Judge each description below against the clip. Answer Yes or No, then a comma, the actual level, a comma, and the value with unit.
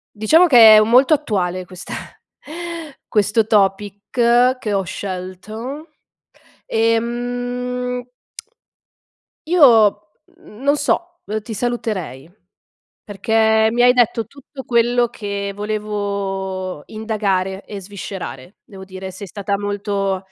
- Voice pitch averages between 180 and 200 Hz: No, high, 215 Hz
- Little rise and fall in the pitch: No, average, 3.6 semitones